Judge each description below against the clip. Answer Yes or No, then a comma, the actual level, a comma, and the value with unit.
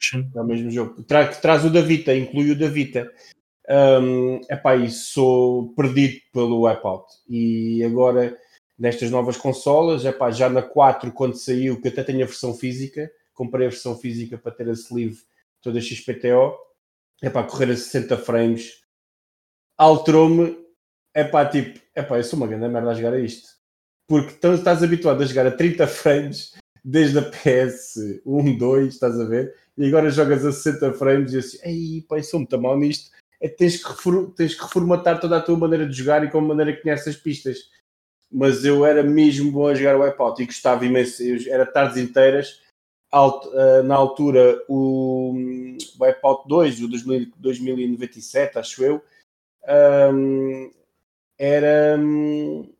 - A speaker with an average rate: Yes, average, 170 wpm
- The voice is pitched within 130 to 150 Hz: Yes, low, 135 Hz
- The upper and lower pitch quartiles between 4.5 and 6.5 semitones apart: No, average, 3.2 semitones